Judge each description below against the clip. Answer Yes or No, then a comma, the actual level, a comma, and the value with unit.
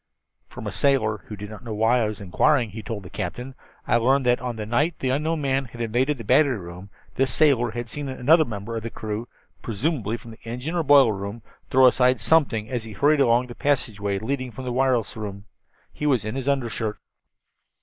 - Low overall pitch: Yes, low, 120 Hz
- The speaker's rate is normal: No, fast, 210 wpm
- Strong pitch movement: No, average, 3.7 semitones